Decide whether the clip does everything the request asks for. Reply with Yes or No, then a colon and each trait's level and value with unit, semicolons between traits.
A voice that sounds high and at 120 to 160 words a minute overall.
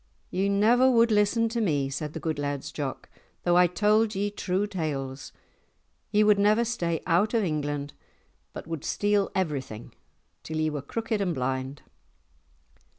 No: medium, 180 Hz; average, 155 wpm